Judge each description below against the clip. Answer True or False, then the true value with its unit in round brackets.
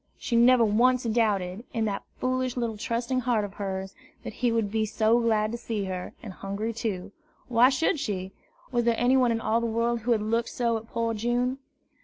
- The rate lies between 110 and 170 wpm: False (200 wpm)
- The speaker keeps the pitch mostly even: True (2.2 semitones)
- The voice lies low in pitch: False (230 Hz)